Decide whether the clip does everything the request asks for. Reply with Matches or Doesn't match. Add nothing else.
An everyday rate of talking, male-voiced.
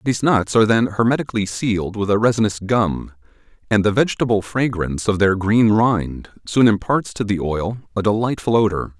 Matches